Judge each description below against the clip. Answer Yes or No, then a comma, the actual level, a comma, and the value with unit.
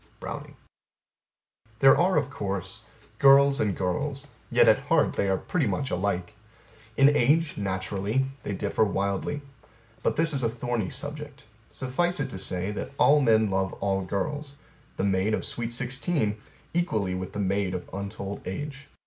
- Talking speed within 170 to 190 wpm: No, average, 155 wpm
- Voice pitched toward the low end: Yes, low, 110 Hz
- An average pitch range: No, wide, 6.3 semitones